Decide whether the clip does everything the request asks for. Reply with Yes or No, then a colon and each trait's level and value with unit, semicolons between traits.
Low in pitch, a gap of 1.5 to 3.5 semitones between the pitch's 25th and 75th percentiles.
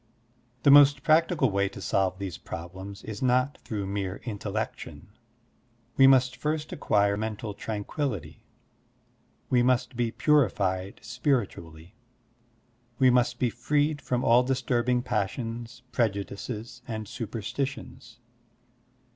No: low, 120 Hz; average, 4.3 semitones